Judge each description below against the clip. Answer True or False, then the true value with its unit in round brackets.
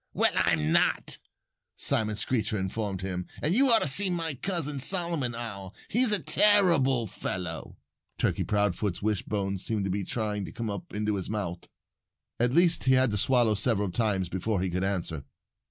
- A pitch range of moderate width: False (5.8 semitones)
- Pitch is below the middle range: True (110 Hz)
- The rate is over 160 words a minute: True (170 wpm)